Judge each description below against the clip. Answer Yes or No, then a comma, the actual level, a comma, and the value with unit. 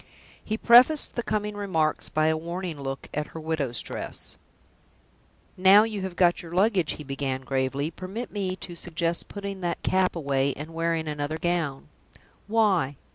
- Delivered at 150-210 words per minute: Yes, average, 160 wpm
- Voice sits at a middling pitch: Yes, medium, 170 Hz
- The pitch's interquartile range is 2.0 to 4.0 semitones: No, average, 4.4 semitones